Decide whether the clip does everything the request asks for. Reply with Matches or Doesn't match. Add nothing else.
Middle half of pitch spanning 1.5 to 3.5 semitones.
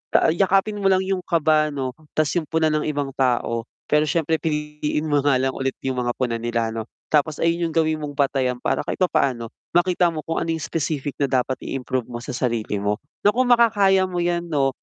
Doesn't match